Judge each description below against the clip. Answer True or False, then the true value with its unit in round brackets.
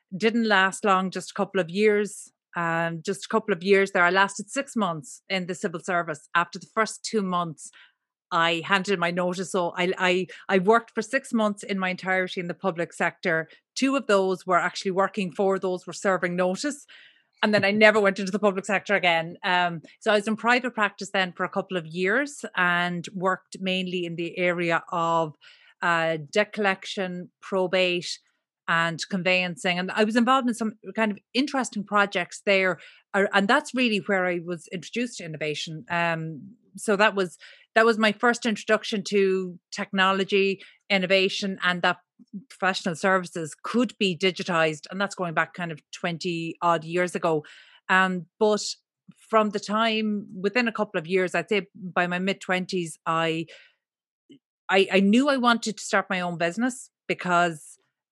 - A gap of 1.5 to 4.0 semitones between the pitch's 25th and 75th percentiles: True (2.9 semitones)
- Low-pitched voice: False (190 Hz)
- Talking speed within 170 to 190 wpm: True (180 wpm)